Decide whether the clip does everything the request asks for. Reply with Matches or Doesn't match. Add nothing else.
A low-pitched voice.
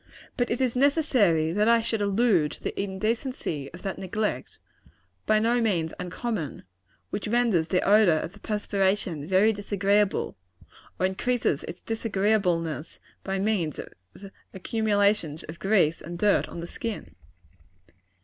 Doesn't match